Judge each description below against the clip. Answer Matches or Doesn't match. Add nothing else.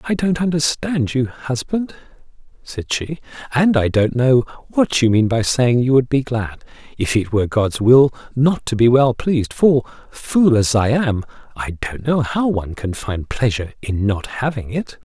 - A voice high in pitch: Doesn't match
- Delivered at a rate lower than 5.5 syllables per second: Matches